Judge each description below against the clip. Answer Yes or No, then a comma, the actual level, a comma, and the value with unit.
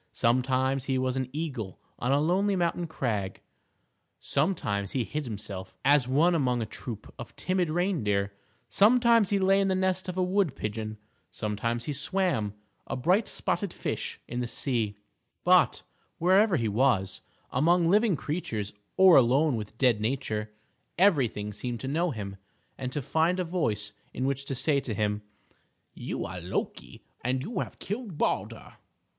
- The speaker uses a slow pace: No, average, 160 wpm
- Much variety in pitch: Yes, wide, 8.0 semitones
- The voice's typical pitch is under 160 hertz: Yes, low, 135 Hz